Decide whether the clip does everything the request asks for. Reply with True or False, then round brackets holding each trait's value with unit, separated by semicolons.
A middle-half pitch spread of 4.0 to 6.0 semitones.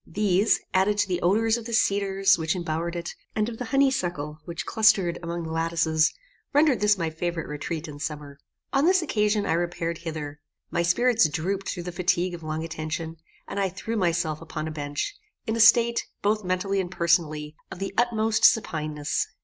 True (4.6 semitones)